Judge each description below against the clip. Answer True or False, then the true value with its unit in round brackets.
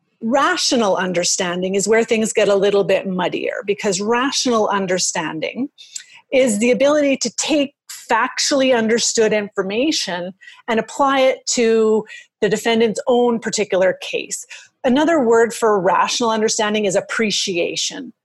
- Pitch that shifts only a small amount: False (4.7 semitones)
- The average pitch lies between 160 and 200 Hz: False (230 Hz)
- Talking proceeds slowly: True (120 wpm)